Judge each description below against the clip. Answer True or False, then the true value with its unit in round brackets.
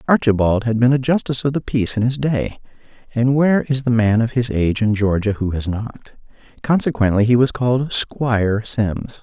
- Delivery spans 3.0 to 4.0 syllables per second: True (3.9 syllables/s)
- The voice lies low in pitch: True (120 Hz)